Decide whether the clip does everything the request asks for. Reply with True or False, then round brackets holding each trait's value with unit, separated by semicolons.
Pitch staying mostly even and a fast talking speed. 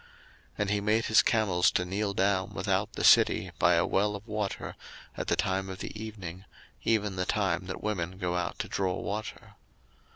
False (2.3 semitones; 195 wpm)